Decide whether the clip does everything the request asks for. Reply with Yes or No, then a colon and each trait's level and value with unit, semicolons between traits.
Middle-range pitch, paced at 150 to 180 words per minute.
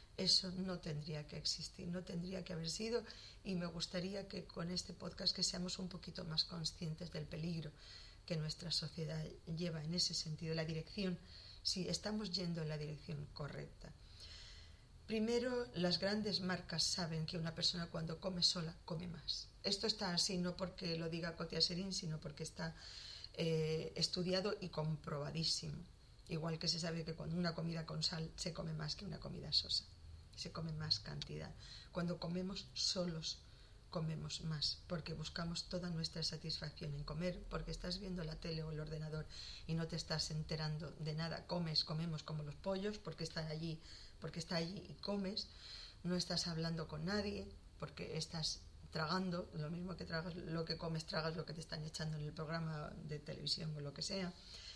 Yes: medium, 165 Hz; average, 175 wpm